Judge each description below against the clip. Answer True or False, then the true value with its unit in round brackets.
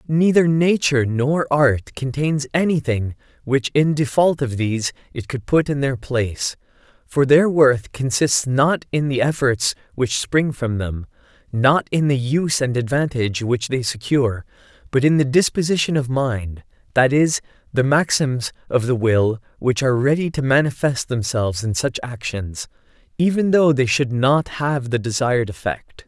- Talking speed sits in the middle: True (160 wpm)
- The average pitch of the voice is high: False (130 Hz)